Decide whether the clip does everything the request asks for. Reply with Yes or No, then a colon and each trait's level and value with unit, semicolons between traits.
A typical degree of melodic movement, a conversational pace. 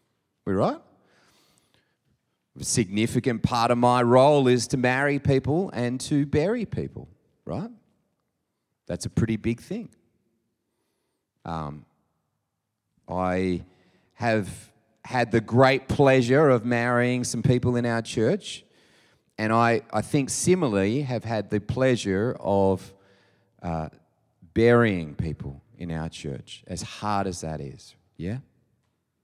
No: average, 4.6 semitones; slow, 120 wpm